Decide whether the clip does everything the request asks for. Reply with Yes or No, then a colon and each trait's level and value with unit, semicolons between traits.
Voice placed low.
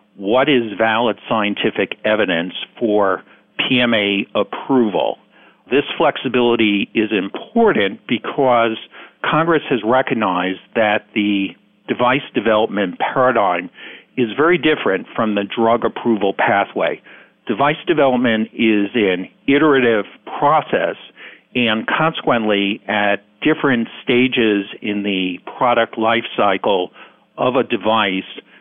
Yes: low, 115 Hz